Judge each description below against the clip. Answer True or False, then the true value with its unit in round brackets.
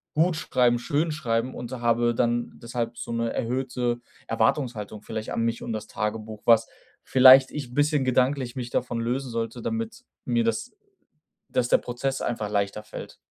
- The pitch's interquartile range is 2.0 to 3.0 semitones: True (2.4 semitones)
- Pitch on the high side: False (120 Hz)